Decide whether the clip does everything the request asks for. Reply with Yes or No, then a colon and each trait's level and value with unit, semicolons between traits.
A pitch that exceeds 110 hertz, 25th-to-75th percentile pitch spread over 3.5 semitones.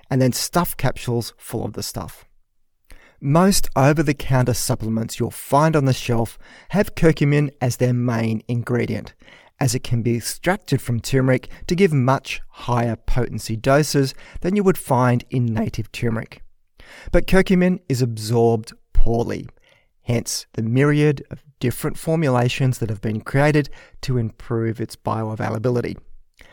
Yes: low, 125 Hz; average, 3.9 semitones